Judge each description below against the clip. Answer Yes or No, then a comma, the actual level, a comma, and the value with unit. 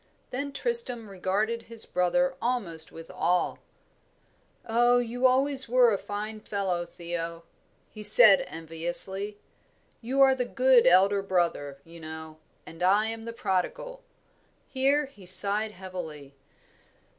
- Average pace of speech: No, slow, 125 wpm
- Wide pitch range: Yes, wide, 5.8 semitones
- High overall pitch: Yes, high, 205 Hz